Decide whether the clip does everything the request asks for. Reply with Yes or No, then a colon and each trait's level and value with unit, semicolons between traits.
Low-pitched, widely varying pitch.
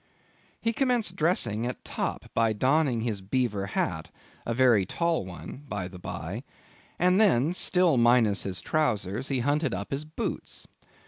Yes: low, 125 Hz; wide, 7.3 semitones